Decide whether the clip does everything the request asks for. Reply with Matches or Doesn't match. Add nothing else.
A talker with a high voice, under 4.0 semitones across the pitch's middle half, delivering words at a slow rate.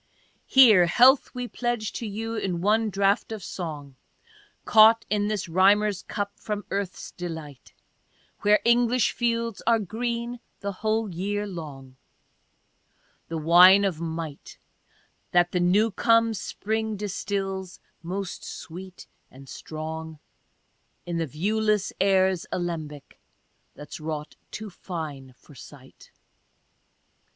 Doesn't match